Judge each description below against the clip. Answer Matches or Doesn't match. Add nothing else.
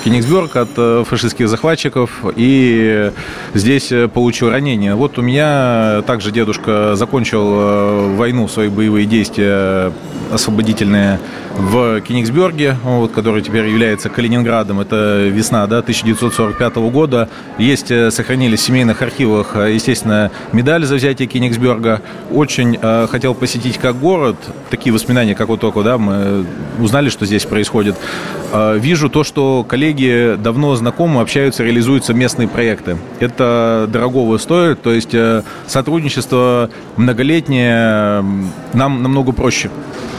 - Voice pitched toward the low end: Matches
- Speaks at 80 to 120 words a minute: Matches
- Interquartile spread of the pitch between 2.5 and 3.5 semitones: Matches